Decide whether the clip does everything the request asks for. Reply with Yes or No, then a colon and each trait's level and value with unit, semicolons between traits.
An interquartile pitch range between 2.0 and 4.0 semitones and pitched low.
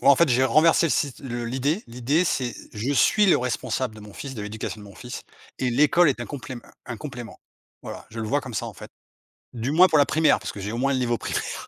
Yes: average, 3.6 semitones; low, 130 Hz